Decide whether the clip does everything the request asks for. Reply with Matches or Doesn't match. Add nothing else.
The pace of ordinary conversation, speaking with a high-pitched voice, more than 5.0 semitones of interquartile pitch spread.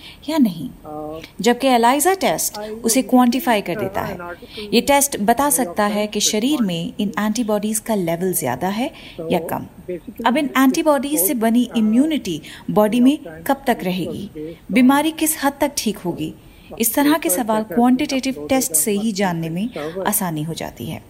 Matches